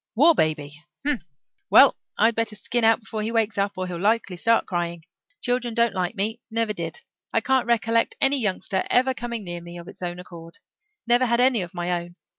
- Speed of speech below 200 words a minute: No, fast, 205 wpm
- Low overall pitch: No, high, 215 Hz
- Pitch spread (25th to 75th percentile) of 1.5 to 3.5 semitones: No, average, 5.2 semitones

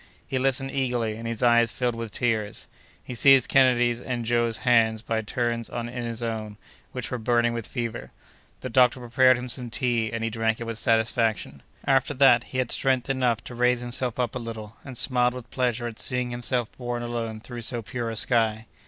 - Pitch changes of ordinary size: No, narrow, 1.7 semitones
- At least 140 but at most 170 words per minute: No, average, 200 wpm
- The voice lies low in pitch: Yes, low, 120 Hz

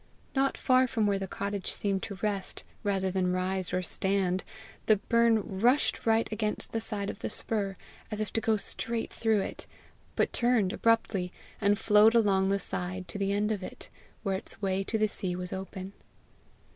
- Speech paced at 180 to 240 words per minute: Yes, average, 185 wpm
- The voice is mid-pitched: No, high, 200 Hz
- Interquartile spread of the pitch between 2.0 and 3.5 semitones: Yes, narrow, 2.6 semitones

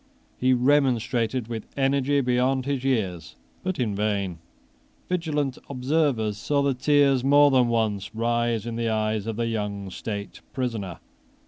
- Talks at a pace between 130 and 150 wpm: Yes, average, 140 wpm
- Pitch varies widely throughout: No, average, 4.0 semitones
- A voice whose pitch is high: No, low, 120 Hz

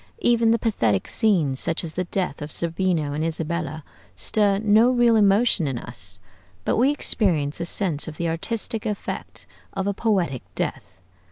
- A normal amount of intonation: No, wide, 5.8 semitones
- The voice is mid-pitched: Yes, medium, 180 Hz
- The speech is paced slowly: No, average, 165 wpm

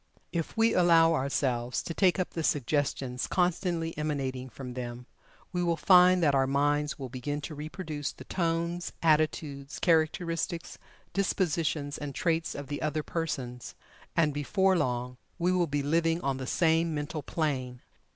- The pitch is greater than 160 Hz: No, medium, 155 Hz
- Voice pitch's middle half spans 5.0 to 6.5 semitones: No, average, 3.4 semitones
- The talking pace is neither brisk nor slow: Yes, average, 150 wpm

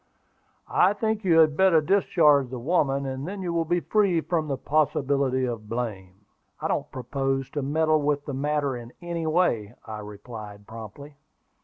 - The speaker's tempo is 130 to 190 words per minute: Yes, average, 170 wpm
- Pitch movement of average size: Yes, average, 5.0 semitones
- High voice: No, medium, 140 Hz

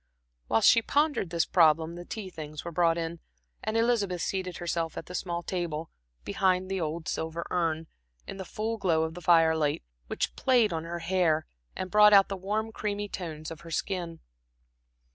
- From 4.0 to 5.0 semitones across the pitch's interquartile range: No, average, 3.2 semitones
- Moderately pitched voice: Yes, medium, 175 Hz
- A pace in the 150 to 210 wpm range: Yes, average, 180 wpm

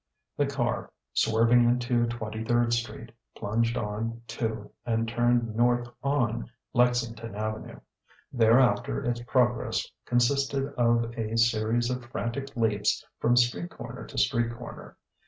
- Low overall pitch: Yes, low, 120 Hz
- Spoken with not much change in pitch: Yes, narrow, 1.2 semitones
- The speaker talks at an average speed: No, slow, 125 wpm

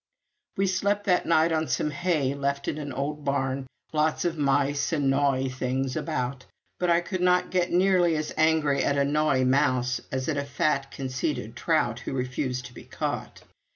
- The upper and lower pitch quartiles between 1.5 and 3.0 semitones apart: No, average, 3.4 semitones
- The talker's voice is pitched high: No, medium, 140 Hz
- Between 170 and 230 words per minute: Yes, average, 185 wpm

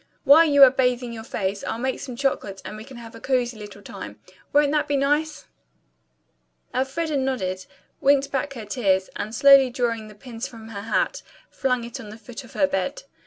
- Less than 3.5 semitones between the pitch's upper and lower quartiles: No, average, 3.9 semitones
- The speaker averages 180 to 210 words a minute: Yes, average, 195 wpm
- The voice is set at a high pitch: Yes, very high, 250 Hz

